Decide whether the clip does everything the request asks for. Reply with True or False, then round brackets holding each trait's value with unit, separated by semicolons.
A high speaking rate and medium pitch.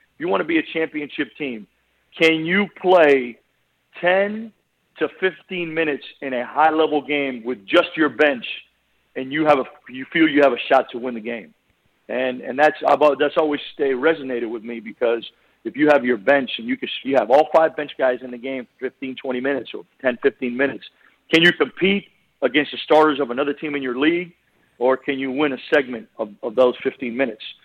True (210 wpm; 145 Hz)